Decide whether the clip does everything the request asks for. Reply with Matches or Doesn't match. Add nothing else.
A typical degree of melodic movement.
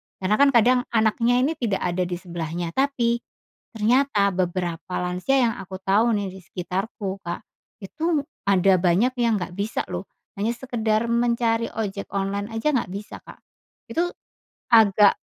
Matches